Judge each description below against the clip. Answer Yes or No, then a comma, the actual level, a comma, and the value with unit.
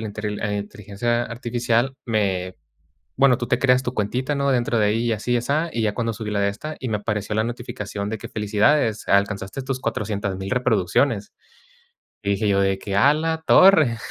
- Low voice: Yes, low, 110 Hz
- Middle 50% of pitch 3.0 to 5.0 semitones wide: Yes, average, 3.5 semitones